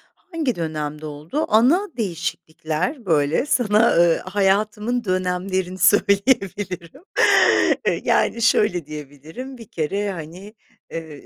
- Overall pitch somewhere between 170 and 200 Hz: Yes, high, 190 Hz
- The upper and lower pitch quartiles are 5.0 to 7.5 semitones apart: Yes, wide, 5.6 semitones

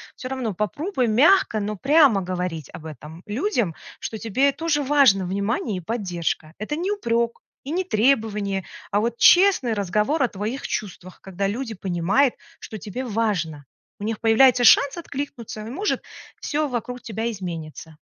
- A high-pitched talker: Yes, high, 225 Hz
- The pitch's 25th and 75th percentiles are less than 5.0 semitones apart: No, wide, 5.6 semitones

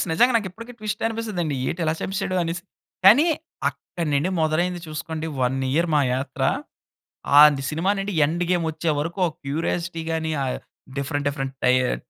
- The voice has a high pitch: No, medium, 165 Hz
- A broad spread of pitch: No, average, 4.2 semitones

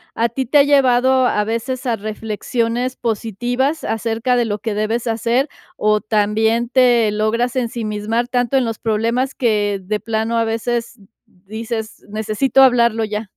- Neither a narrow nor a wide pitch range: No, narrow, 2.2 semitones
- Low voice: No, high, 230 Hz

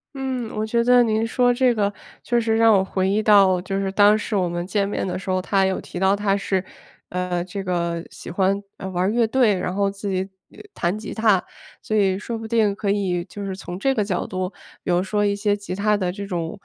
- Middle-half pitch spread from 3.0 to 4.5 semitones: No, narrow, 2.6 semitones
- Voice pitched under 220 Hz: Yes, high, 200 Hz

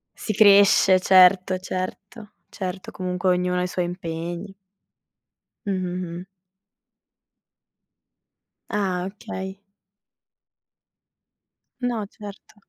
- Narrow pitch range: Yes, narrow, 1.7 semitones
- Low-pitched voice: No, medium, 185 Hz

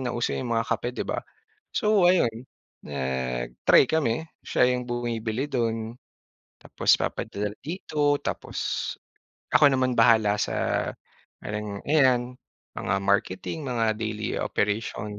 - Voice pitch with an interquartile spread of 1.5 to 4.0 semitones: Yes, average, 3.6 semitones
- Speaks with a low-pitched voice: Yes, low, 115 Hz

